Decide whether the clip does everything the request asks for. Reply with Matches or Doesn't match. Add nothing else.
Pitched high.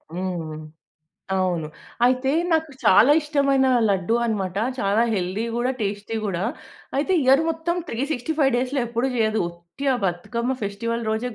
Matches